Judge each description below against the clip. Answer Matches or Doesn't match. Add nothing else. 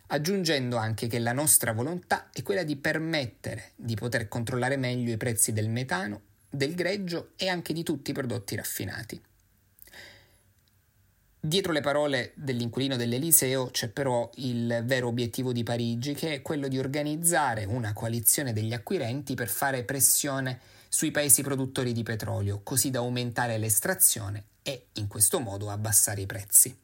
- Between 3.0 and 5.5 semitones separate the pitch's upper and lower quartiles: Matches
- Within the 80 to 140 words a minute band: Doesn't match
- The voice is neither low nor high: Doesn't match